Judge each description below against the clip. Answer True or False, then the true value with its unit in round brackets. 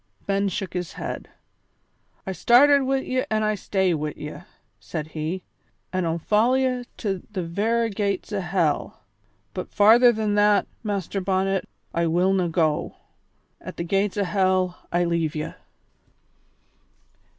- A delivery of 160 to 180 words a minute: False (145 wpm)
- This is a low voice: False (195 Hz)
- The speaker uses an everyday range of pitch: True (3.7 semitones)